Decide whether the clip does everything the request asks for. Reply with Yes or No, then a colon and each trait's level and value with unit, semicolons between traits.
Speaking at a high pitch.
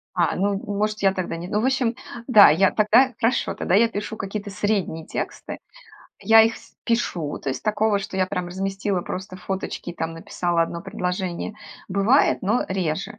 Yes: high, 195 Hz